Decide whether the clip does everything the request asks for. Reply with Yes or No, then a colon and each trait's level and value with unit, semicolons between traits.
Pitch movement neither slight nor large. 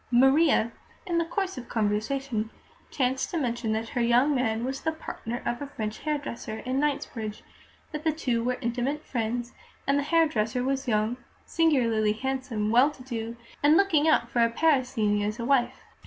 Yes: average, 4.0 semitones